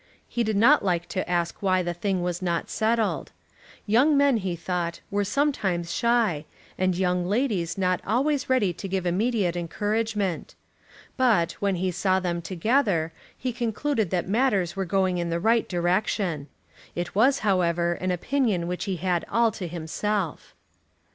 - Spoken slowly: No, average, 160 wpm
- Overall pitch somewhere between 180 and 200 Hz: Yes, high, 190 Hz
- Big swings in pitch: No, average, 4.3 semitones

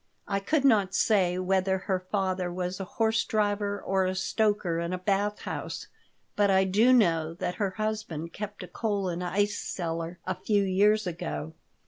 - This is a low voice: No, high, 190 Hz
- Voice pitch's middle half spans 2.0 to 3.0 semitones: Yes, narrow, 2.5 semitones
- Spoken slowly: No, average, 175 wpm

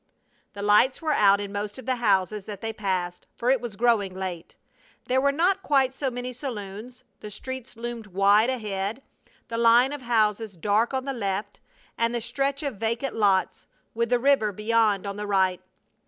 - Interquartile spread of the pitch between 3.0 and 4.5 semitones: Yes, average, 3.9 semitones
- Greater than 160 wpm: Yes, average, 185 wpm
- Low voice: No, high, 225 Hz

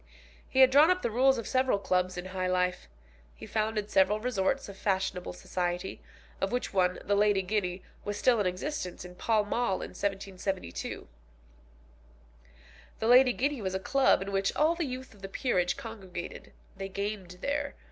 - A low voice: No, high, 200 Hz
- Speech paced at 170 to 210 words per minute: Yes, average, 175 wpm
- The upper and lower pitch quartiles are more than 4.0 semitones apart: Yes, average, 5.0 semitones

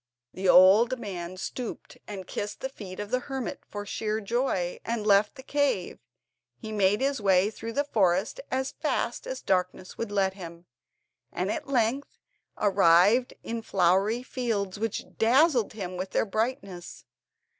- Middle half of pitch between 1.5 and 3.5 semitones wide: No, average, 4.5 semitones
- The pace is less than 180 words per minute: Yes, average, 155 wpm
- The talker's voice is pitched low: No, high, 210 Hz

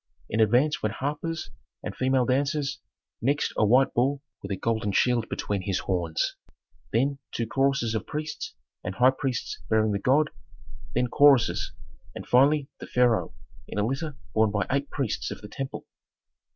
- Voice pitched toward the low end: Yes, low, 125 Hz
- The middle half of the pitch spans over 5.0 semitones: No, average, 4.2 semitones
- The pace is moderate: Yes, average, 165 wpm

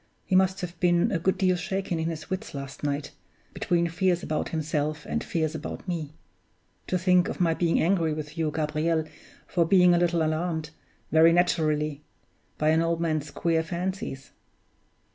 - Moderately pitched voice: Yes, medium, 165 Hz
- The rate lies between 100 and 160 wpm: No, average, 170 wpm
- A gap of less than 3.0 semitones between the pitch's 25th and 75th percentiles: Yes, narrow, 2.4 semitones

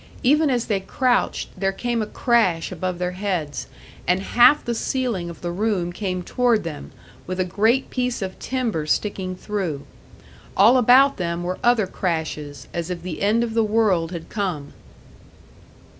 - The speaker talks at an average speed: Yes, average, 165 wpm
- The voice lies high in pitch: Yes, high, 195 Hz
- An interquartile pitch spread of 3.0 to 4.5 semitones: No, average, 5.2 semitones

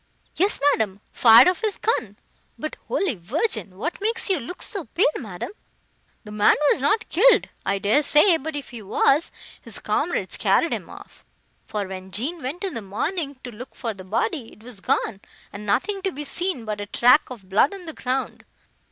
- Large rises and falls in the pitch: Yes, wide, 8.8 semitones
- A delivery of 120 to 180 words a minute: No, average, 190 wpm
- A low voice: No, very high, 260 Hz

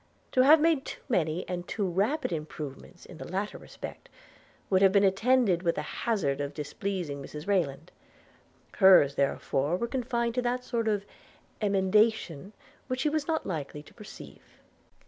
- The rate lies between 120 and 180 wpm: Yes, average, 160 wpm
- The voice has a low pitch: No, high, 195 Hz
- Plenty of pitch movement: Yes, wide, 6.9 semitones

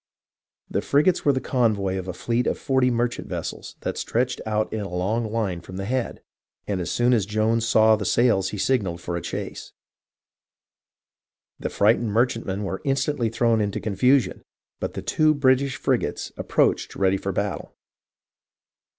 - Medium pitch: No, low, 110 Hz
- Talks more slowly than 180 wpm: Yes, average, 165 wpm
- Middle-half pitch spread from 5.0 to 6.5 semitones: No, average, 4.2 semitones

